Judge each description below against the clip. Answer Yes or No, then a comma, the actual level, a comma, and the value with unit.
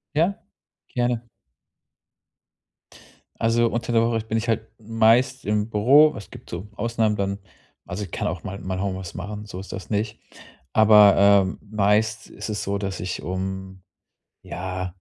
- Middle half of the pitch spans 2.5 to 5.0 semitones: Yes, average, 2.9 semitones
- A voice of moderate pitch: No, low, 105 Hz